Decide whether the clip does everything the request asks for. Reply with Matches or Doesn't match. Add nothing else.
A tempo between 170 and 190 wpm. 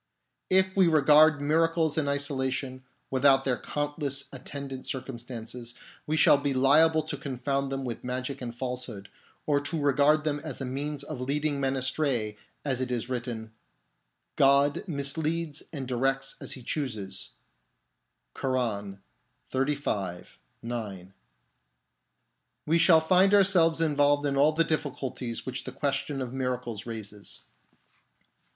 Doesn't match